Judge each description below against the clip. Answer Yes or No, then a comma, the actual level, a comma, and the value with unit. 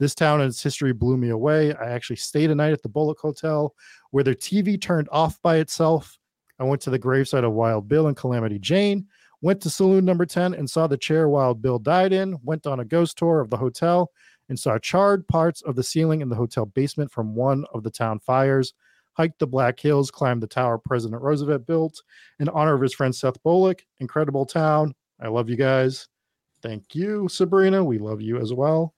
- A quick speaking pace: Yes, fast, 215 wpm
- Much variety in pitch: No, average, 4.1 semitones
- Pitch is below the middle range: No, medium, 145 Hz